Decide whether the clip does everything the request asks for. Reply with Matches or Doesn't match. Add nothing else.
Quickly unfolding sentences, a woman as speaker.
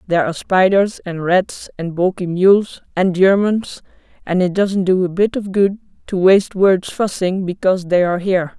Doesn't match